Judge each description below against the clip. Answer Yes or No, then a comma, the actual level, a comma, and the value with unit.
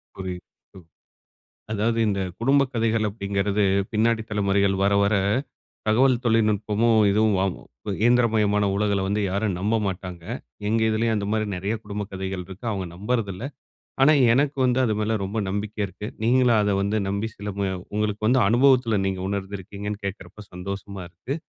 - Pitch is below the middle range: Yes, low, 105 Hz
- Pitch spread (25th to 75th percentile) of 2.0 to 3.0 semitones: Yes, narrow, 2.4 semitones